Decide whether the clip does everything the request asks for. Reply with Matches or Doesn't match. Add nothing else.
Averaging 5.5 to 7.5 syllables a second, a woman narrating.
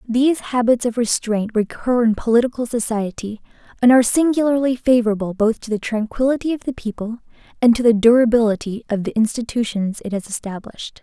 Matches